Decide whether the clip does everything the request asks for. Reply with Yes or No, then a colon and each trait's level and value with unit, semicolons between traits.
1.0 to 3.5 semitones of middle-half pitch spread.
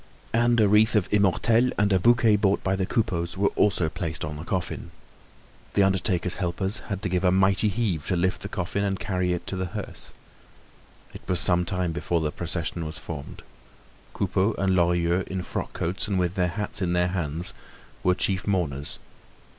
Yes: narrow, 2.5 semitones